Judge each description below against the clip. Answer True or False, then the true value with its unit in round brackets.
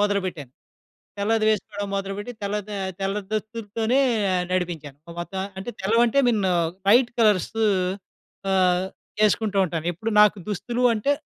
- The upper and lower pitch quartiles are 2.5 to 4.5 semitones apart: True (2.9 semitones)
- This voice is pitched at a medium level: False (205 Hz)